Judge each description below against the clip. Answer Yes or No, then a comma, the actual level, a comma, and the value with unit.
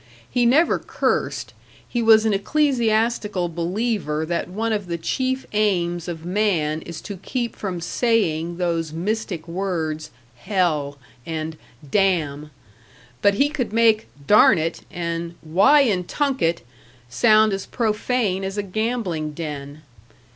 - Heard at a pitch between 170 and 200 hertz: Yes, high, 190 Hz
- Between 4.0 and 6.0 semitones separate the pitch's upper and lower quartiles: Yes, average, 5.1 semitones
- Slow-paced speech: Yes, slow, 130 wpm